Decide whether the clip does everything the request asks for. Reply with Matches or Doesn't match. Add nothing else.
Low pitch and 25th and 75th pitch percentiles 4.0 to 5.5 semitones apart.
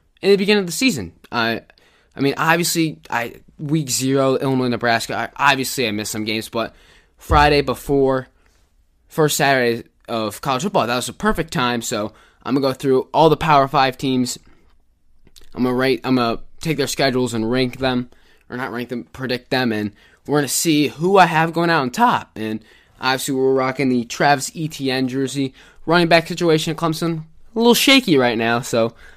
Matches